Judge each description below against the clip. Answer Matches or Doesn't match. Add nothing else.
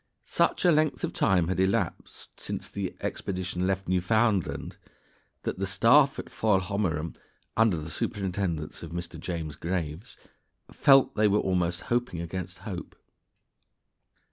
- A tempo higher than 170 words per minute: Doesn't match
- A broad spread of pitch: Doesn't match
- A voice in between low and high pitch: Doesn't match